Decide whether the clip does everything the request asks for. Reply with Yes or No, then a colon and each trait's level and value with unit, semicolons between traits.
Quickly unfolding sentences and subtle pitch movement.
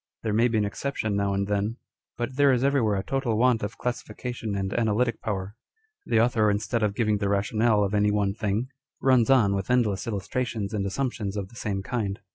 No: fast, 210 wpm; average, 3.0 semitones